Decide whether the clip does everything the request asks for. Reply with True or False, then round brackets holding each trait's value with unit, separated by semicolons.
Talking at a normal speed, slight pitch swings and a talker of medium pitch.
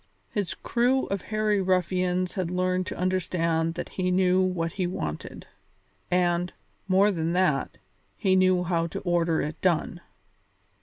True (145 wpm; 1.6 semitones; 180 Hz)